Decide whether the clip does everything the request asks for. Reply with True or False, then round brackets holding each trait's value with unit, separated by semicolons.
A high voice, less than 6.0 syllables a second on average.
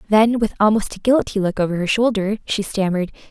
False (205 Hz; 6.1 syllables/s)